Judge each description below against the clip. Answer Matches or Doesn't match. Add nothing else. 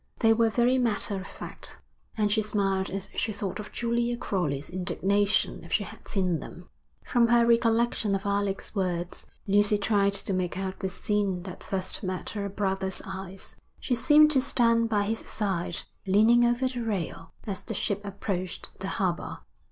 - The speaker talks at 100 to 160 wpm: Doesn't match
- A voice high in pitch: Matches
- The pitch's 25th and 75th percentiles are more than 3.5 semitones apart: Doesn't match